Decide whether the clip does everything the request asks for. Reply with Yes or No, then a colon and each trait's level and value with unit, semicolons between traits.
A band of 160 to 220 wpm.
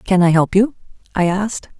Yes: average, 200 wpm